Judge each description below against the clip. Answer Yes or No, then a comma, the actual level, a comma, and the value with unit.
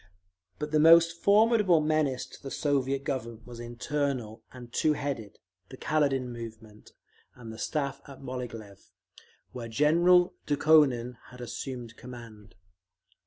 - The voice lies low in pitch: Yes, low, 130 Hz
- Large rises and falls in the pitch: No, average, 4.3 semitones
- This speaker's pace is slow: Yes, slow, 120 wpm